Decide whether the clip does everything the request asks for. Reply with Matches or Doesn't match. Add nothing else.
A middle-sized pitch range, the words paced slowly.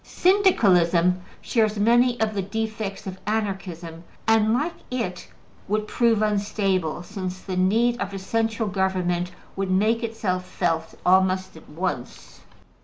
Matches